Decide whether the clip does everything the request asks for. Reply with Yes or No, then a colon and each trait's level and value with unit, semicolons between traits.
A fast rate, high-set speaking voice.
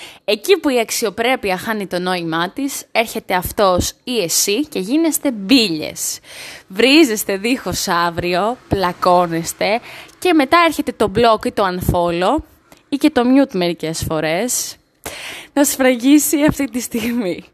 No: average, 130 wpm; high, 230 Hz